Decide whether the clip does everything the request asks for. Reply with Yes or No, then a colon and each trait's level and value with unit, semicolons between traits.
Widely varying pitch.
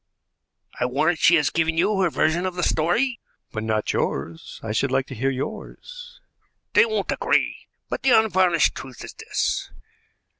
Yes: wide, 6.9 semitones